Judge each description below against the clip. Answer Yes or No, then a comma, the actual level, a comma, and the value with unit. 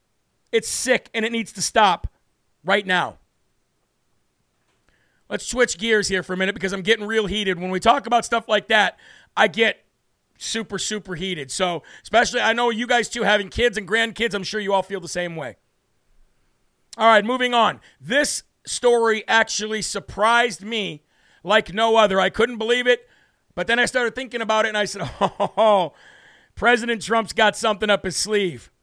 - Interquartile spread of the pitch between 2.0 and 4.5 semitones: Yes, average, 3.3 semitones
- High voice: Yes, high, 220 Hz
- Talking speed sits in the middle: Yes, average, 180 wpm